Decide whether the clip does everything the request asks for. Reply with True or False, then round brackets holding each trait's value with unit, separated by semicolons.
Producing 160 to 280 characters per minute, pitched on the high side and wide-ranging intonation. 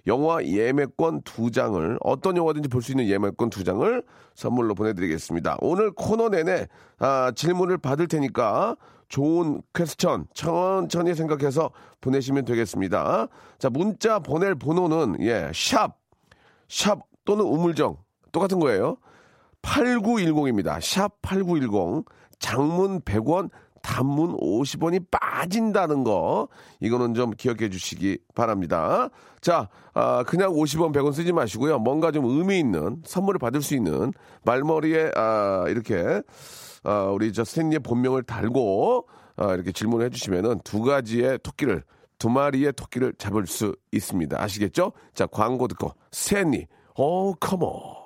False (270 characters per minute; 140 Hz; 6.6 semitones)